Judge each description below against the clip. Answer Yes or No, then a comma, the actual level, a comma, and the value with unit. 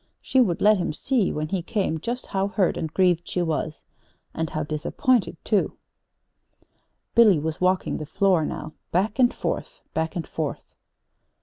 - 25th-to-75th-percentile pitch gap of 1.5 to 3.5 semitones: No, average, 4.7 semitones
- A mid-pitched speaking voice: Yes, medium, 180 Hz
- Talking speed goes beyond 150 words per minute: Yes, average, 165 wpm